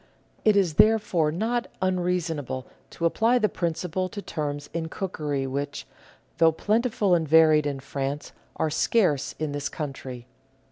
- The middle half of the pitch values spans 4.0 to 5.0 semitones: Yes, average, 4.5 semitones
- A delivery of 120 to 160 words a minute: Yes, average, 145 wpm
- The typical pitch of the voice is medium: Yes, medium, 160 Hz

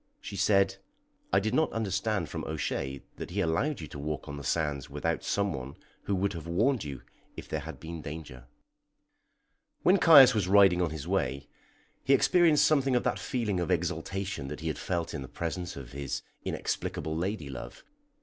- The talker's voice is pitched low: Yes, very low, 90 Hz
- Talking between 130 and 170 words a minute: No, average, 190 wpm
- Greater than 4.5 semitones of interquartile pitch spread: Yes, wide, 5.5 semitones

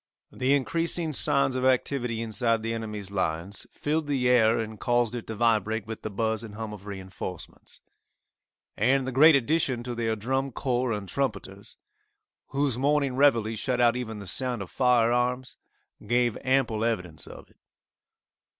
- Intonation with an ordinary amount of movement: Yes, average, 3.2 semitones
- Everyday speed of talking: Yes, average, 160 wpm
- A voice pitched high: No, low, 120 Hz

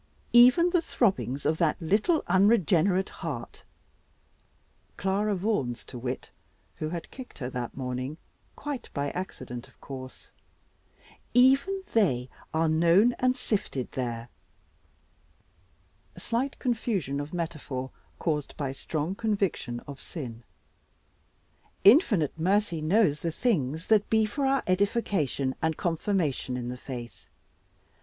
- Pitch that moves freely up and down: Yes, wide, 7.9 semitones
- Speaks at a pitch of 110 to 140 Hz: No, medium, 165 Hz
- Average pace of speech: No, slow, 120 wpm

